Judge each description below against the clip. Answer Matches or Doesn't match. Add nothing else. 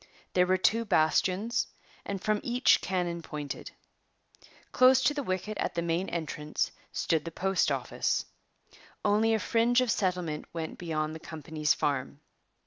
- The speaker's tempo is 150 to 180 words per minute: Doesn't match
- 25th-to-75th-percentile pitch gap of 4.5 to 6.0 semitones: Matches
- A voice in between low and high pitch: Matches